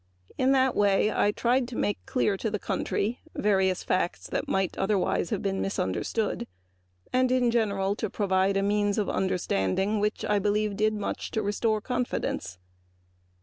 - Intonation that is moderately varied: No, narrow, 2.0 semitones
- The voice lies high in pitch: Yes, high, 205 Hz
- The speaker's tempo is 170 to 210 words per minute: No, average, 150 wpm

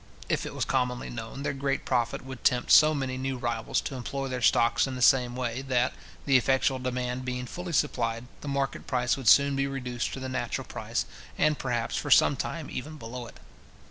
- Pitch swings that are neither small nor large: No, narrow, 1.8 semitones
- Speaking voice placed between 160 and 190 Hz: No, low, 130 Hz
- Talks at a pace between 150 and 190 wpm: No, fast, 205 wpm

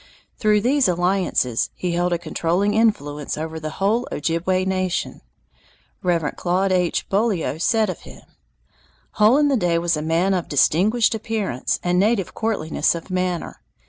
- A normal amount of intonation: Yes, average, 4.0 semitones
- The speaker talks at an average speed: Yes, average, 150 wpm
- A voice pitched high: No, medium, 180 Hz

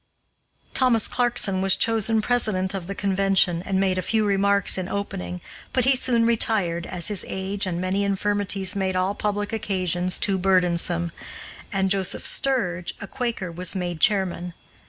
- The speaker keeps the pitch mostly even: Yes, narrow, 2.2 semitones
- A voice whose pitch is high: Yes, high, 195 Hz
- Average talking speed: Yes, average, 155 wpm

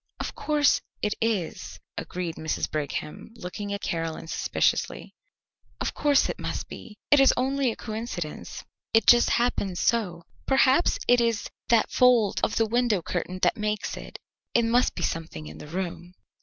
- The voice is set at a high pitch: Yes, high, 215 Hz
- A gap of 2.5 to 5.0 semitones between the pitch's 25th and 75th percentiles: No, wide, 5.6 semitones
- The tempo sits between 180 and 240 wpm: No, average, 160 wpm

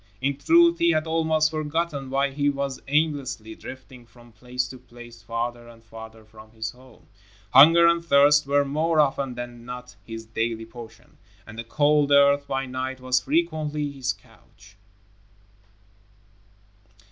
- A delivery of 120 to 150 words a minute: Yes, average, 145 wpm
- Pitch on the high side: No, low, 135 Hz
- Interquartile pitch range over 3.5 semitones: Yes, average, 3.9 semitones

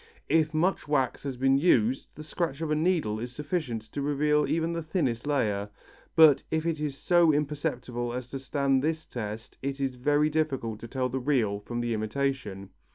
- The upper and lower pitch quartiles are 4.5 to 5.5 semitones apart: No, average, 4.1 semitones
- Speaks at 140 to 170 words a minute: No, average, 190 wpm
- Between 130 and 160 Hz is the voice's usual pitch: Yes, medium, 140 Hz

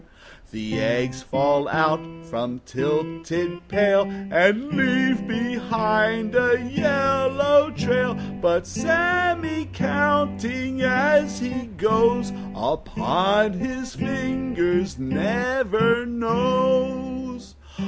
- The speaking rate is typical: No, slow, 80 wpm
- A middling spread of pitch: No, wide, 6.7 semitones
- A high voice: Yes, high, 230 Hz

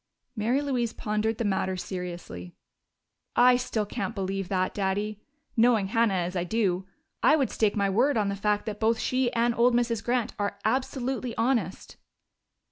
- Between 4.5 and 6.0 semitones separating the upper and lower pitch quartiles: No, average, 3.6 semitones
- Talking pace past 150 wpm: Yes, average, 165 wpm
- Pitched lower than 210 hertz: No, high, 215 Hz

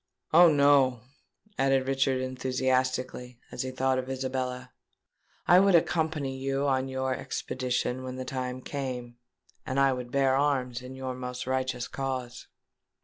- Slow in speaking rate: No, average, 145 wpm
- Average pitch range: No, narrow, 1.1 semitones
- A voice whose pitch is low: Yes, low, 130 Hz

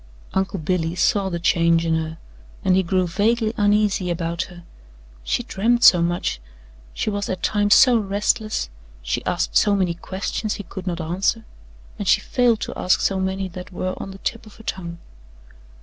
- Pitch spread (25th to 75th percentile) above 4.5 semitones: No, average, 3.3 semitones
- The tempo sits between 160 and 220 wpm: Yes, average, 180 wpm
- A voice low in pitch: No, high, 190 Hz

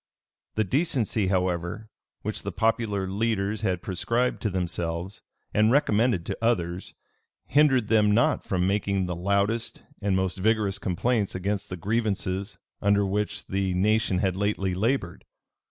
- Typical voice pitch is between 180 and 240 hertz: No, low, 100 Hz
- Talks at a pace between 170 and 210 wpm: No, average, 140 wpm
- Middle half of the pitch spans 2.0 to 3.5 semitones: Yes, average, 2.9 semitones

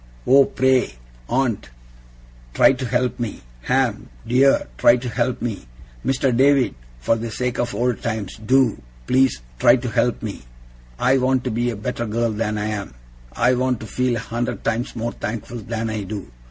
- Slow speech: No, average, 180 wpm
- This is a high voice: No, low, 120 Hz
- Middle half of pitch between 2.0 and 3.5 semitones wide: Yes, average, 2.7 semitones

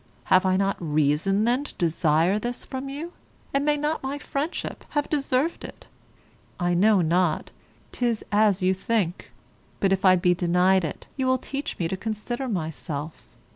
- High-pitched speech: Yes, high, 195 Hz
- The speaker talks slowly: No, average, 170 wpm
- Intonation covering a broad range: Yes, wide, 6.6 semitones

